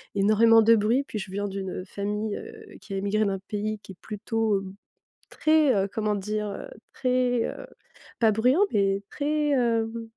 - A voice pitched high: Yes, high, 215 Hz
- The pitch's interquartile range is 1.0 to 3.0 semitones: Yes, narrow, 2.5 semitones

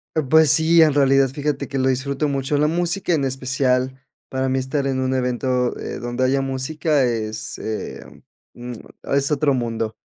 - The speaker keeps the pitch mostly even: Yes, narrow, 2.1 semitones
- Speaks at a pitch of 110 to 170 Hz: Yes, low, 135 Hz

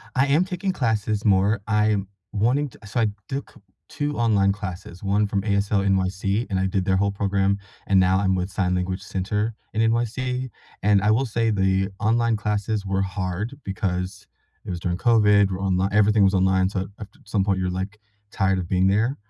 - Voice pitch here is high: No, low, 100 Hz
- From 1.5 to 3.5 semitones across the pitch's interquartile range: Yes, narrow, 2.5 semitones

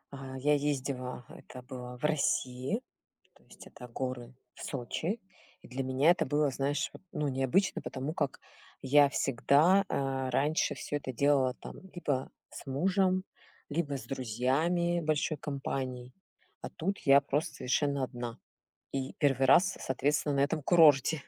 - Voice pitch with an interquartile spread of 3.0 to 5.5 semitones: No, narrow, 2.6 semitones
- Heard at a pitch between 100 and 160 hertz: Yes, medium, 140 Hz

